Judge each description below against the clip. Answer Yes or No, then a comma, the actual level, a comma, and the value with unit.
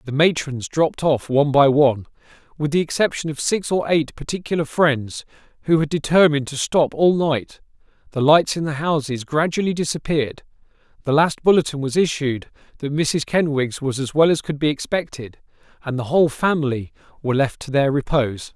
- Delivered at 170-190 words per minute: Yes, average, 175 wpm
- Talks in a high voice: No, medium, 150 Hz